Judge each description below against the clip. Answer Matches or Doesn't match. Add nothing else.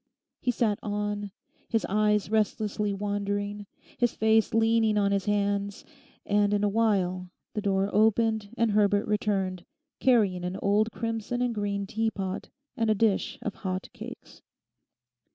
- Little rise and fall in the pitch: Matches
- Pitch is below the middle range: Doesn't match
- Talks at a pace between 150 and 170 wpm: Doesn't match